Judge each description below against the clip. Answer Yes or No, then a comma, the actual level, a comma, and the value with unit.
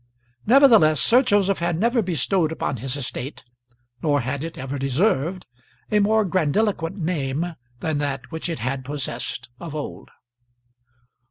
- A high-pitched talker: No, medium, 160 Hz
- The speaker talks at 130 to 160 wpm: Yes, average, 140 wpm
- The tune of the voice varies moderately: No, wide, 6.0 semitones